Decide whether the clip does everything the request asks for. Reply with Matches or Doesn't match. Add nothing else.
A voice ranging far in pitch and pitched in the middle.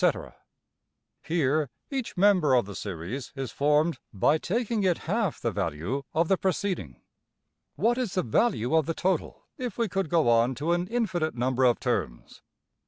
Matches